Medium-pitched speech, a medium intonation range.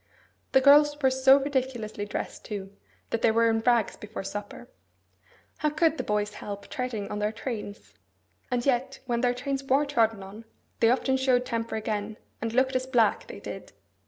No: high, 240 Hz; average, 3.7 semitones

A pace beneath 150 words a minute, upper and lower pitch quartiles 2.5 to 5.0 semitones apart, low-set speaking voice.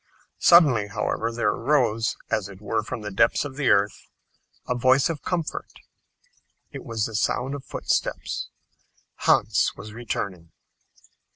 Yes: slow, 135 wpm; average, 4.1 semitones; low, 115 Hz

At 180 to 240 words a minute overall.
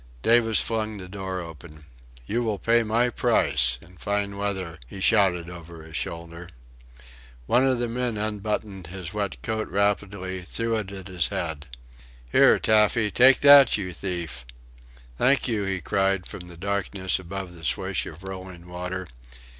No: average, 155 wpm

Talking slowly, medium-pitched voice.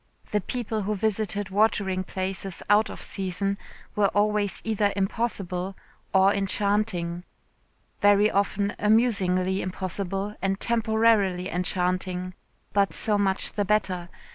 No: slow, 115 wpm; high, 200 Hz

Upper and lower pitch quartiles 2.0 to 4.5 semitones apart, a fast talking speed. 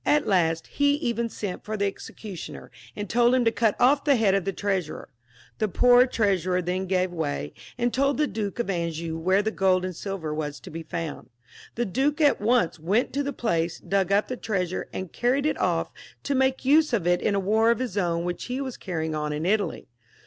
No: wide, 5.6 semitones; fast, 220 wpm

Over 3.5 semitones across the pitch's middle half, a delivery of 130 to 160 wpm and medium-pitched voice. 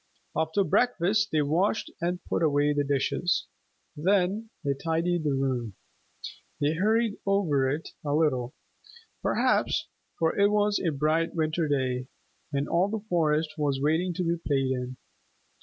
Yes: average, 4.1 semitones; average, 145 wpm; medium, 160 Hz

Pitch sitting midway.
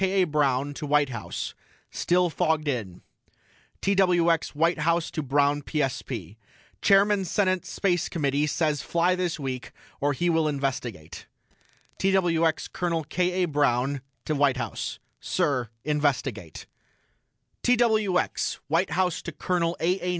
Yes: medium, 160 Hz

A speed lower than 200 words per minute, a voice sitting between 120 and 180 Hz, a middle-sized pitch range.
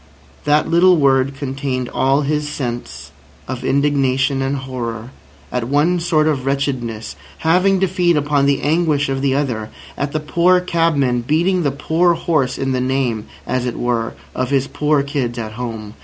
Yes: average, 165 wpm; medium, 140 Hz; average, 3.2 semitones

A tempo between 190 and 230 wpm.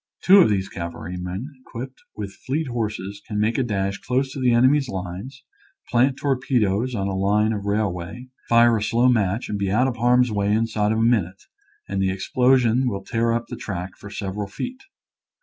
Yes: average, 195 wpm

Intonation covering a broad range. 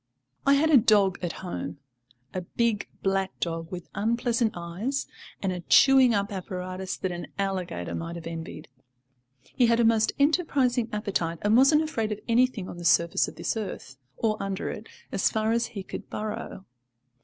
No: average, 4.5 semitones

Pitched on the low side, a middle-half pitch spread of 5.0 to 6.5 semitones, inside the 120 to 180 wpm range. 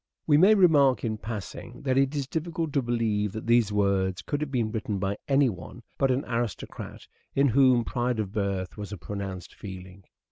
No: low, 115 Hz; wide, 5.4 semitones; average, 190 wpm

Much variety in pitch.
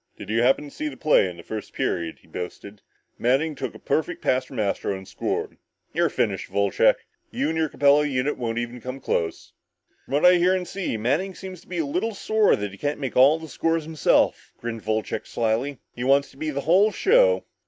Yes: wide, 6.1 semitones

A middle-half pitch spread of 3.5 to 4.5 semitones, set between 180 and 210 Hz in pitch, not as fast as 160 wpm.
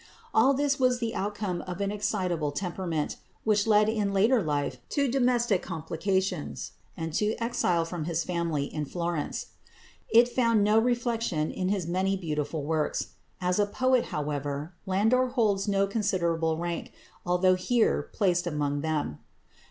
No: average, 5.1 semitones; high, 190 Hz; average, 145 wpm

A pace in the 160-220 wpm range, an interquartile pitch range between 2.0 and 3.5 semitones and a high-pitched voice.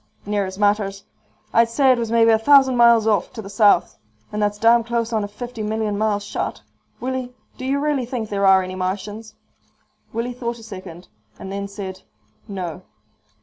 Yes: average, 190 wpm; average, 2.9 semitones; high, 215 Hz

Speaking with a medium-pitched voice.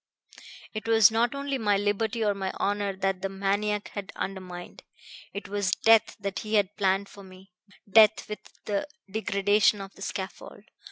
No: high, 205 Hz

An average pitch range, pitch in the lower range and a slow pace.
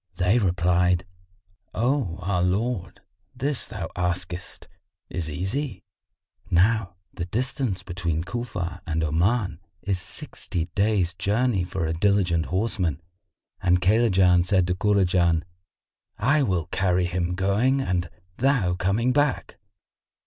Yes: average, 3.7 semitones; very low, 90 Hz; slow, 115 wpm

